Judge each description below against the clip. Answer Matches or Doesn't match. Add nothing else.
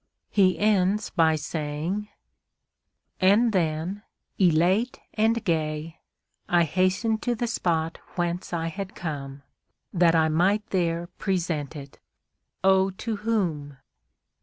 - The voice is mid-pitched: Matches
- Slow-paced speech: Matches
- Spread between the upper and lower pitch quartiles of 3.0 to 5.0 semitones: Matches